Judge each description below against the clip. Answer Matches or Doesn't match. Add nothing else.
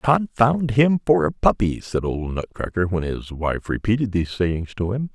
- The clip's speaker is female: Doesn't match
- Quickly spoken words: Doesn't match